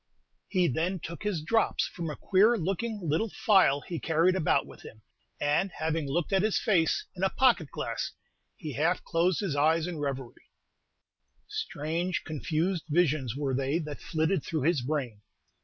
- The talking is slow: No, average, 165 wpm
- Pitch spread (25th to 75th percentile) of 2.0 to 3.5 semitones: No, average, 3.9 semitones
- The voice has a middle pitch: Yes, medium, 165 Hz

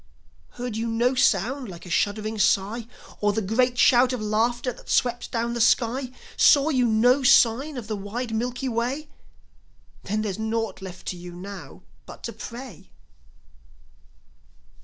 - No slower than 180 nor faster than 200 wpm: No, average, 155 wpm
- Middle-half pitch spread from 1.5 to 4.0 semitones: Yes, average, 2.8 semitones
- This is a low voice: No, high, 230 Hz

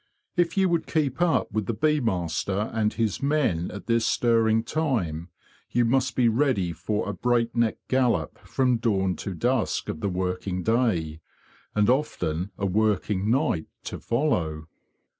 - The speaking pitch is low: Yes, low, 110 Hz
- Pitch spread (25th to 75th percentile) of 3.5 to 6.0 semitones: Yes, wide, 5.5 semitones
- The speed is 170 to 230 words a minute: No, average, 160 wpm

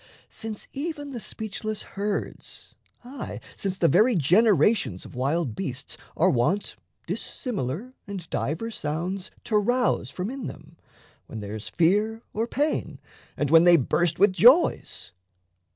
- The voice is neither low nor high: No, high, 195 Hz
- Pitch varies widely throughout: Yes, wide, 6.0 semitones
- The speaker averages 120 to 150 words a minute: Yes, slow, 135 wpm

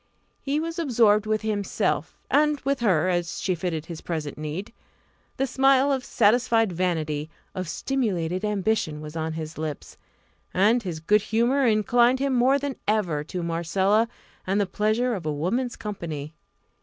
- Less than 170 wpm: Yes, average, 155 wpm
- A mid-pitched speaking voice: No, high, 205 Hz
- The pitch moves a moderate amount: No, wide, 6.5 semitones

